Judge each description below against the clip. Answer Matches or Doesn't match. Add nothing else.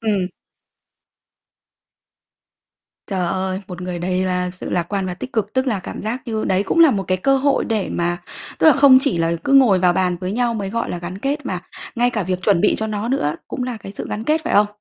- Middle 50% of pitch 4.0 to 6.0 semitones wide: Matches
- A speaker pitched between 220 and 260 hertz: Doesn't match